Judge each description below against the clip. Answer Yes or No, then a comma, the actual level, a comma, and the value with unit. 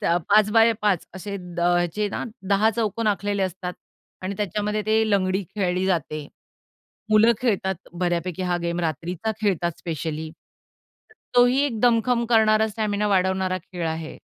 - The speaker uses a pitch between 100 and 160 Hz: No, high, 195 Hz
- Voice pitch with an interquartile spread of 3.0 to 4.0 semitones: Yes, average, 3.4 semitones